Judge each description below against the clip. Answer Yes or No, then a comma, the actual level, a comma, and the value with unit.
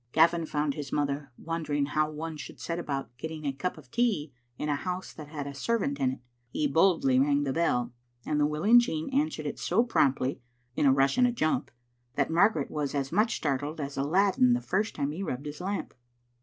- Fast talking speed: Yes, fast, 210 wpm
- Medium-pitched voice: Yes, medium, 150 Hz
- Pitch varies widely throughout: No, average, 3.5 semitones